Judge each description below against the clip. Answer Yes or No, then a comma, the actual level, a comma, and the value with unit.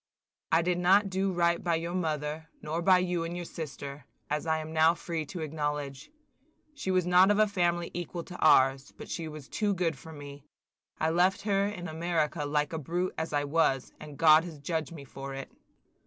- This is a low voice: No, medium, 165 Hz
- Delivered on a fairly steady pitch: No, average, 3.0 semitones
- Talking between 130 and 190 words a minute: No, fast, 205 wpm